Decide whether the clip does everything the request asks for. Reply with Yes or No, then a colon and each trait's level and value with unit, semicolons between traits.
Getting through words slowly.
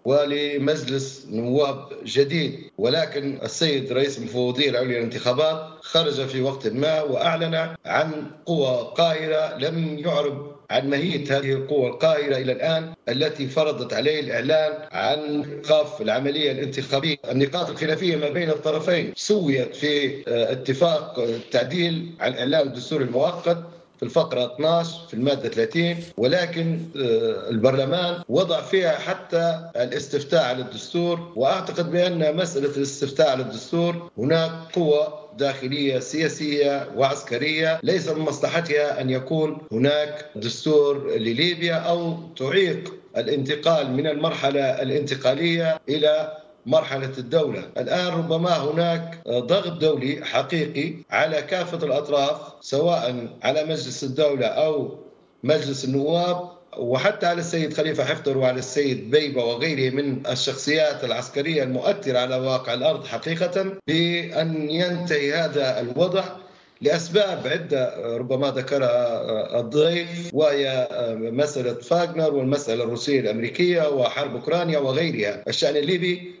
Yes: slow, 110 wpm